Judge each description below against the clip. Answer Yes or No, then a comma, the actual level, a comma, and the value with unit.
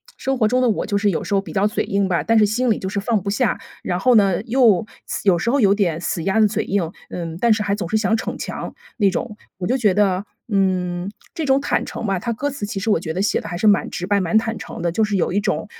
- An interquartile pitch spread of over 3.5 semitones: No, average, 2.9 semitones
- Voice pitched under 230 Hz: Yes, high, 205 Hz